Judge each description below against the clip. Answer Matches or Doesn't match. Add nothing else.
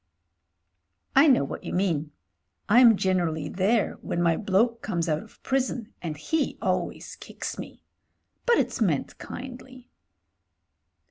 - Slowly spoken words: Matches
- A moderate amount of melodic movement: Doesn't match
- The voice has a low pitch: Doesn't match